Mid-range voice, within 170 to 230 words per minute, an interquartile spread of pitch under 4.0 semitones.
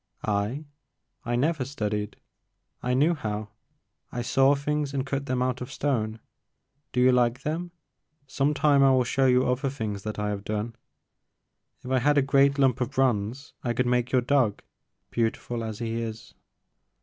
No: low, 125 Hz; average, 175 wpm; average, 3.5 semitones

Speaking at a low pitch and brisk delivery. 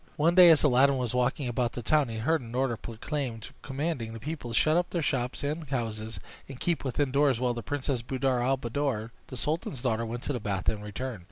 Yes: low, 130 Hz; fast, 230 wpm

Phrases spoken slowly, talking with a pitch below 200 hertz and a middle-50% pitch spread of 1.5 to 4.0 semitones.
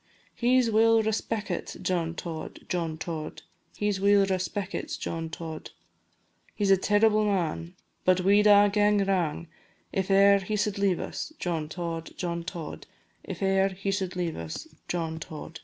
No: average, 165 wpm; high, 190 Hz; average, 3.4 semitones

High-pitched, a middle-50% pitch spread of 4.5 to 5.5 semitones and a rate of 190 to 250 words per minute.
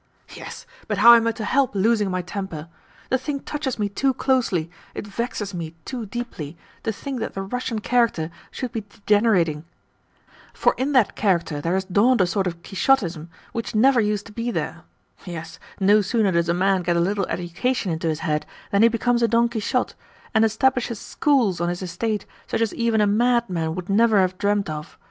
Yes: high, 205 Hz; average, 4.8 semitones; average, 195 wpm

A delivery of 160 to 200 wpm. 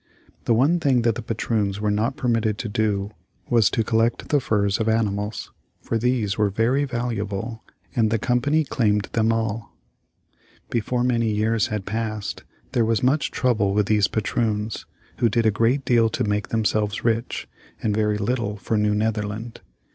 Yes: average, 170 wpm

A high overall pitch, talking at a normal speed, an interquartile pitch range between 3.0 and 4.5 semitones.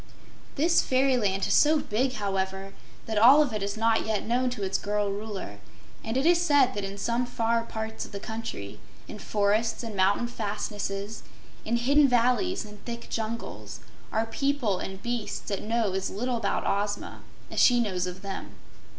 Yes: high, 220 Hz; average, 175 wpm; average, 3.4 semitones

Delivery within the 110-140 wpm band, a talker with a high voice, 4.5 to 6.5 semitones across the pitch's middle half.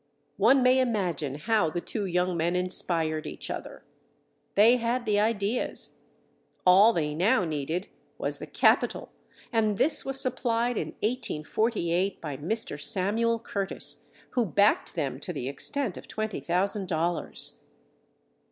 Yes: slow, 135 wpm; high, 200 Hz; average, 5.1 semitones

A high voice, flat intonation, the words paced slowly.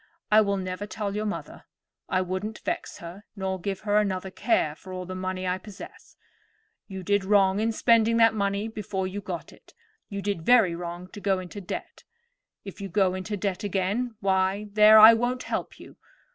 No: high, 200 Hz; narrow, 2.2 semitones; average, 190 wpm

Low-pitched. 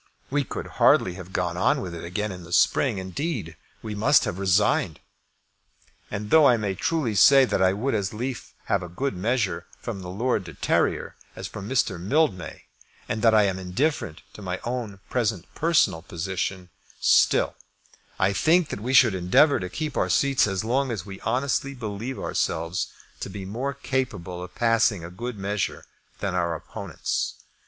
Yes: low, 100 Hz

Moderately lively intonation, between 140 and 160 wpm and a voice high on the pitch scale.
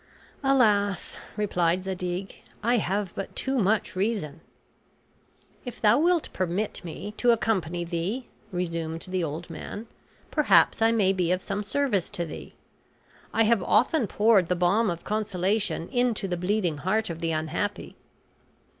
Yes: average, 4.1 semitones; average, 145 wpm; high, 195 Hz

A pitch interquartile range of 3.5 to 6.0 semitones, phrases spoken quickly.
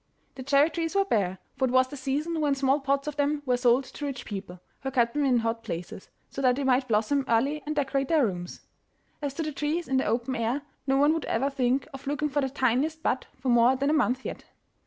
No: average, 2.9 semitones; fast, 245 wpm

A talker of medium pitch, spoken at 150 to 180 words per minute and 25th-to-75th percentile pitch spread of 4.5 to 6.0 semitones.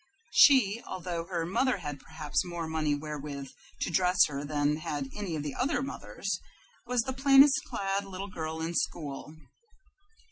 Yes: medium, 170 Hz; average, 155 wpm; average, 5.0 semitones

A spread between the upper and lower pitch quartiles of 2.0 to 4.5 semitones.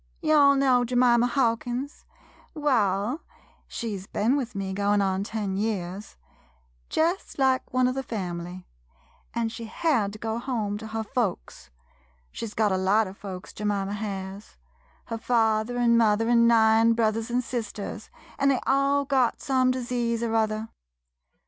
Yes: average, 3.5 semitones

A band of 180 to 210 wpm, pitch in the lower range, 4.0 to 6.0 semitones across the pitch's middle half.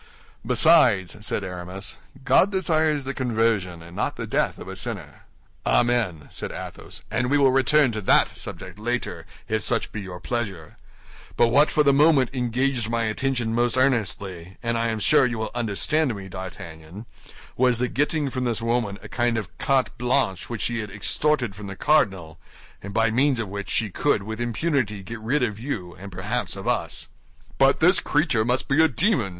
Yes: average, 185 wpm; low, 115 Hz; average, 5.1 semitones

